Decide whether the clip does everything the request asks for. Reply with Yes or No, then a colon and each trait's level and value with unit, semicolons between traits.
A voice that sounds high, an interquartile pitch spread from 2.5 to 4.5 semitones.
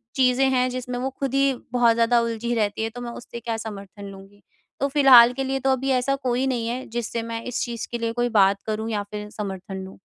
Yes: high, 235 Hz; average, 2.8 semitones